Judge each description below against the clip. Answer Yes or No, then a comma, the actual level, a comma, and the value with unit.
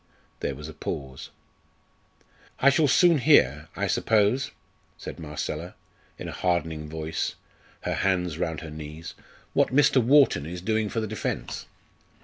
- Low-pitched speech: Yes, very low, 85 Hz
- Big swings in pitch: Yes, wide, 6.7 semitones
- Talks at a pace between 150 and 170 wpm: No, average, 140 wpm